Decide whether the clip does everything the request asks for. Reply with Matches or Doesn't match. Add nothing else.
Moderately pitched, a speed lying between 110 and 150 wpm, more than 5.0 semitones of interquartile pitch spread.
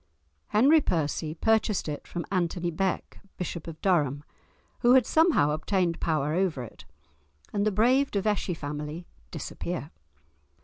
Matches